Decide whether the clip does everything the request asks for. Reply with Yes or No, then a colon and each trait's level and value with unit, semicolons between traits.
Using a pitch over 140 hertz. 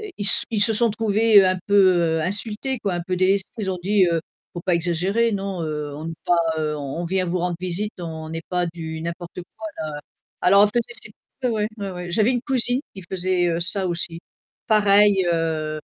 Yes: medium, 185 Hz